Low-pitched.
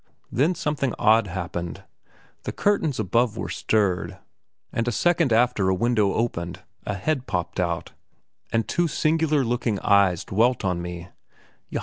Yes: low, 110 Hz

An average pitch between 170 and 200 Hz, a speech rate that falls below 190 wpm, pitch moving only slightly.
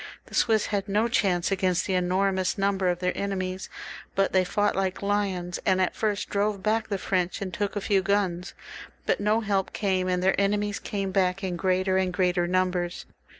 No: high, 190 Hz; average, 195 wpm; narrow, 1.7 semitones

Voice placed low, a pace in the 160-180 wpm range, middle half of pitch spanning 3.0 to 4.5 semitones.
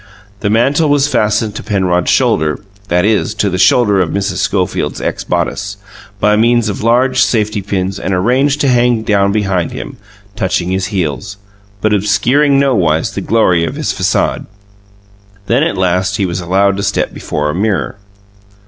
Yes: low, 100 Hz; average, 165 wpm; average, 3.7 semitones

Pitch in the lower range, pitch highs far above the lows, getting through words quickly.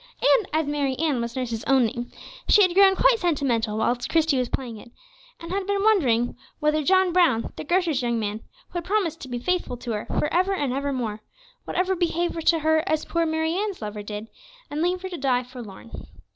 No: very high, 300 Hz; wide, 6.6 semitones; fast, 215 wpm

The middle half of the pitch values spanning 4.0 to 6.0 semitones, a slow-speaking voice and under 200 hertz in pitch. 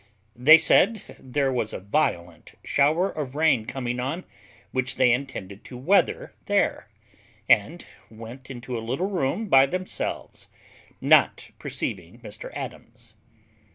Yes: average, 4.4 semitones; slow, 125 wpm; low, 135 Hz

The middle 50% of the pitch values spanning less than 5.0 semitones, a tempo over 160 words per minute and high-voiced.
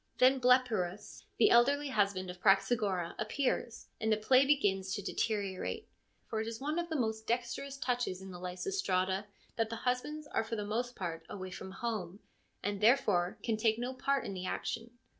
Yes: average, 4.6 semitones; average, 180 wpm; high, 220 Hz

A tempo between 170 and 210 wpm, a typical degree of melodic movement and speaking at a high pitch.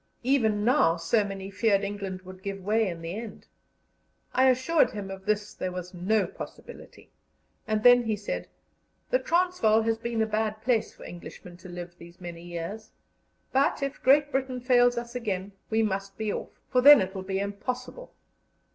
Yes: average, 180 wpm; average, 4.3 semitones; high, 215 Hz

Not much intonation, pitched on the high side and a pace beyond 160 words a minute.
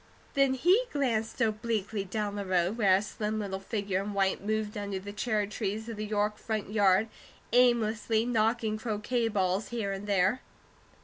Yes: narrow, 2.1 semitones; high, 215 Hz; average, 170 wpm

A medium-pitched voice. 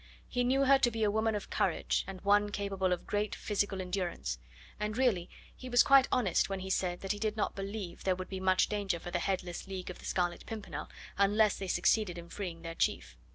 No: high, 195 Hz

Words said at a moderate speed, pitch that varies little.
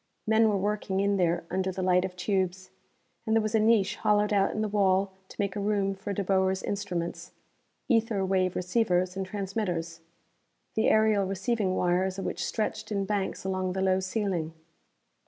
Yes: average, 180 wpm; narrow, 1.9 semitones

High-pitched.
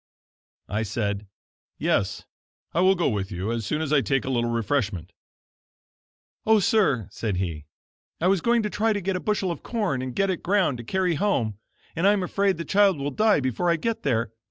No: medium, 155 Hz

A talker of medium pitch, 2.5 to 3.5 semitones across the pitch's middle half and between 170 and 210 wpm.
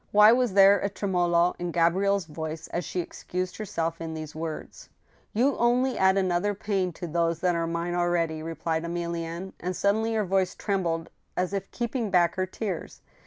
Yes: medium, 180 Hz; average, 3.0 semitones; average, 185 wpm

